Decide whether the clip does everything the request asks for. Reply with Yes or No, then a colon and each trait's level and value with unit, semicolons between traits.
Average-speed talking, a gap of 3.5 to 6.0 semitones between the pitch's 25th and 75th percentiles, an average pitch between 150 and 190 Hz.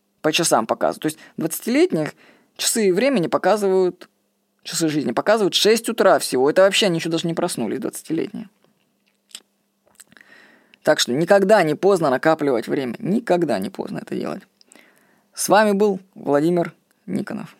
Yes: average, 135 wpm; average, 5.1 semitones; medium, 185 Hz